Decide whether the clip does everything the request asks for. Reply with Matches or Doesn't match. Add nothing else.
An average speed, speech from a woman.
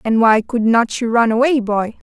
Doesn't match